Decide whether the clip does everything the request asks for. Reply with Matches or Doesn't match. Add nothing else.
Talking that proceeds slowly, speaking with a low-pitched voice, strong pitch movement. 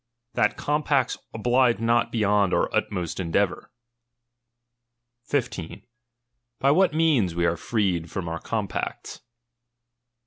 Matches